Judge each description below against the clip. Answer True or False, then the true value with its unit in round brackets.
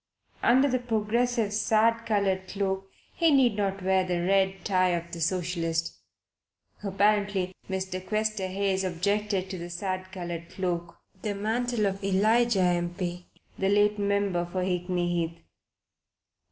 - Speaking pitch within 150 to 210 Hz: True (190 Hz)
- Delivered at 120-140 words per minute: True (135 wpm)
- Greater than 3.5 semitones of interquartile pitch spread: False (2.6 semitones)